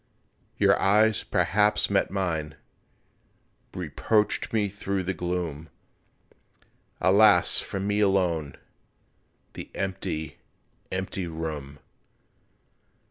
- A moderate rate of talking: No, slow, 80 wpm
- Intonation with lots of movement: No, average, 3.8 semitones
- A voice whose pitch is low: Yes, very low, 95 Hz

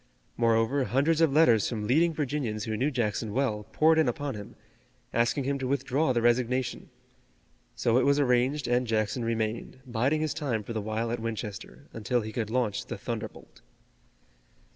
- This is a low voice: Yes, low, 120 Hz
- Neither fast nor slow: Yes, average, 170 wpm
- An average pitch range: Yes, average, 3.7 semitones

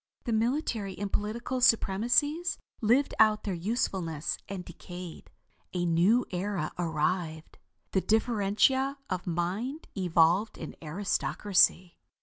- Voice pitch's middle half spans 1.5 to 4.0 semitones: No, average, 4.7 semitones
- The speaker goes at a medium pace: No, slow, 110 wpm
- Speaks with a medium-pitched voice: No, high, 195 Hz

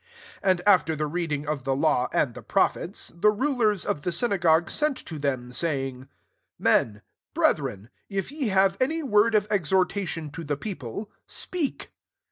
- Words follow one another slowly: No, average, 160 wpm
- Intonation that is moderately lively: No, wide, 6.2 semitones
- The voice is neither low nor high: Yes, medium, 175 Hz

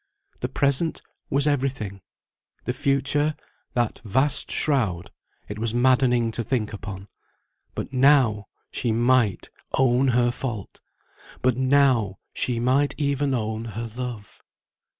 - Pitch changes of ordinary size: Yes, average, 3.5 semitones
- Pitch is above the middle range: No, low, 125 Hz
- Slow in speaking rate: Yes, slow, 120 wpm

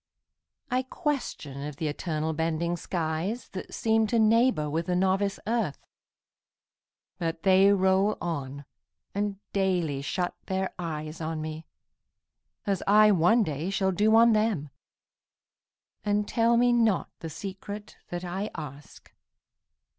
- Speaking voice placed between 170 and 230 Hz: Yes, high, 190 Hz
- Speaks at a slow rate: Yes, slow, 130 wpm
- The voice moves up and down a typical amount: Yes, average, 4.9 semitones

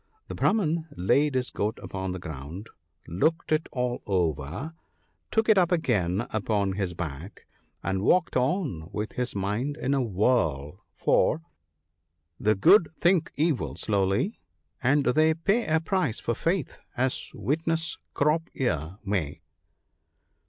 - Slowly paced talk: No, average, 150 wpm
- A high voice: No, low, 120 Hz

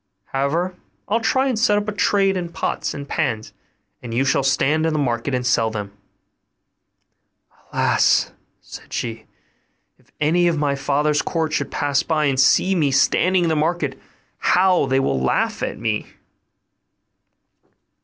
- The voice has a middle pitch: Yes, medium, 150 Hz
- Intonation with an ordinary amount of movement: Yes, average, 4.7 semitones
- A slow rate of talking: No, average, 155 wpm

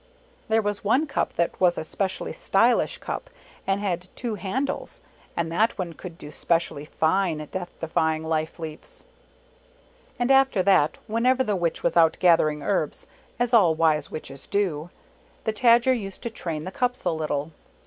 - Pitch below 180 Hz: No, medium, 185 Hz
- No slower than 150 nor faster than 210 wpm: Yes, average, 170 wpm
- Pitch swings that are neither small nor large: No, wide, 5.7 semitones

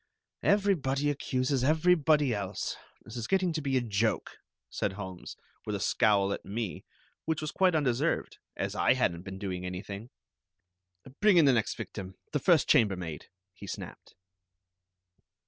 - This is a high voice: No, low, 125 Hz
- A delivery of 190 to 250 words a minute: No, average, 145 wpm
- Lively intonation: Yes, wide, 7.6 semitones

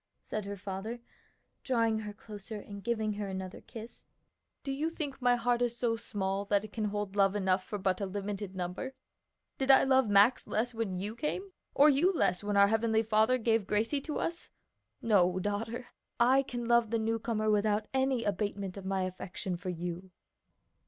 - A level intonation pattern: No, average, 3.2 semitones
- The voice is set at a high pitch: Yes, high, 215 Hz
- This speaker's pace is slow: No, average, 185 wpm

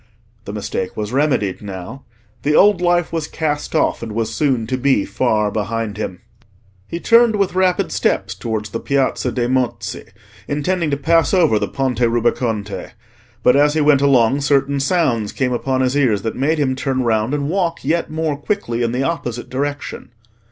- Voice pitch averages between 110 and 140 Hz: Yes, low, 135 Hz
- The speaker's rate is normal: Yes, average, 180 wpm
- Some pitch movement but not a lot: Yes, average, 4.8 semitones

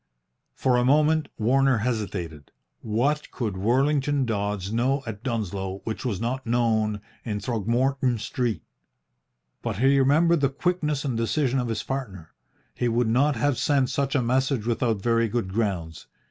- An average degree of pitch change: Yes, average, 4.0 semitones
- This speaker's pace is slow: No, average, 150 wpm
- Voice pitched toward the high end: No, low, 120 Hz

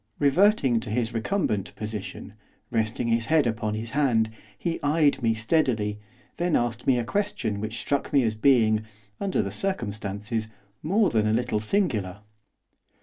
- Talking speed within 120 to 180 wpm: Yes, average, 150 wpm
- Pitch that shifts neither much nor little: Yes, average, 5.0 semitones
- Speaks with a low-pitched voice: Yes, low, 115 Hz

